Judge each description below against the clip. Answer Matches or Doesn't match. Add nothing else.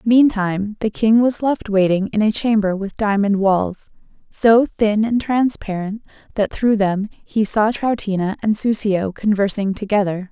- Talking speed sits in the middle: Matches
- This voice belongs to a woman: Matches